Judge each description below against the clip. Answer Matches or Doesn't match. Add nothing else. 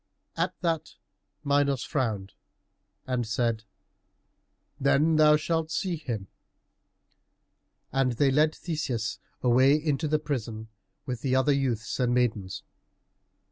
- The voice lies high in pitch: Doesn't match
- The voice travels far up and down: Doesn't match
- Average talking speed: Doesn't match